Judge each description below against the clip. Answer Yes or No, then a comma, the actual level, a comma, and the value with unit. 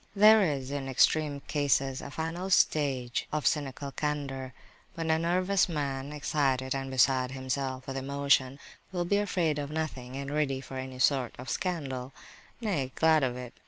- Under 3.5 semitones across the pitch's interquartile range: Yes, average, 3.1 semitones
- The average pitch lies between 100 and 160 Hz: Yes, medium, 140 Hz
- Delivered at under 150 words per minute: No, average, 160 wpm